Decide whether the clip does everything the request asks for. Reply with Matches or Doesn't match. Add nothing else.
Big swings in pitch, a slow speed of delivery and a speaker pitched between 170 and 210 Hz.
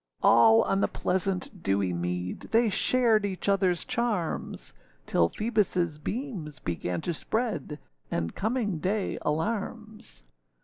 Matches